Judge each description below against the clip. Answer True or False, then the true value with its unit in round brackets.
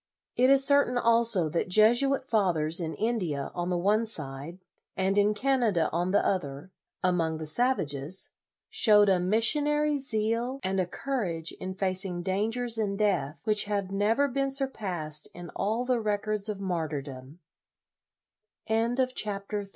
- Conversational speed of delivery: False (125 wpm)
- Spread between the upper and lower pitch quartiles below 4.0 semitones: False (5.3 semitones)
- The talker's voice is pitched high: True (205 Hz)